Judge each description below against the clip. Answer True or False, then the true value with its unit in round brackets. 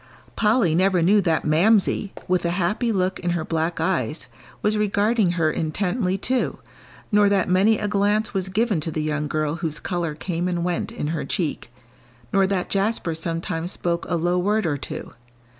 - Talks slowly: False (180 wpm)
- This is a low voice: False (180 Hz)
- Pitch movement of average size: True (3.7 semitones)